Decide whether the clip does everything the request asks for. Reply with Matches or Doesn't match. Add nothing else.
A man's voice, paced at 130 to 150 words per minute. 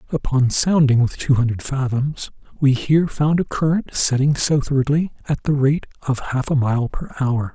Doesn't match